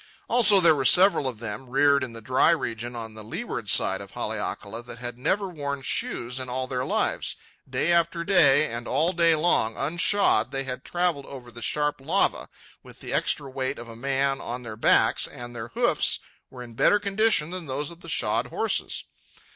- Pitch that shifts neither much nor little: No, wide, 5.7 semitones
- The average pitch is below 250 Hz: Yes, low, 135 Hz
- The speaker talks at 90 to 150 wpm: No, average, 195 wpm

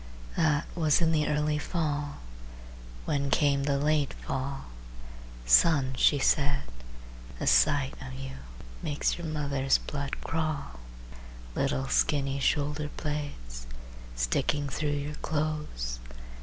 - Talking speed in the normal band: No, slow, 115 wpm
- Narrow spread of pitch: Yes, narrow, 2.0 semitones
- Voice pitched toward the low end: No, medium, 145 Hz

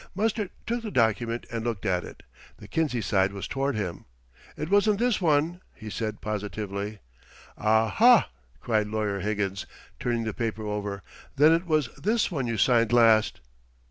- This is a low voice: Yes, low, 115 Hz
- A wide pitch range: Yes, wide, 6.9 semitones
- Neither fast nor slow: Yes, average, 165 wpm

